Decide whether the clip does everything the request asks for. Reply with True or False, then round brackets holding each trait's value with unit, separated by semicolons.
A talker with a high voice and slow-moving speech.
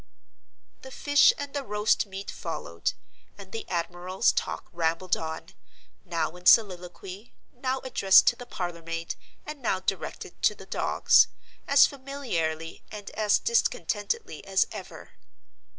True (195 Hz; 125 wpm)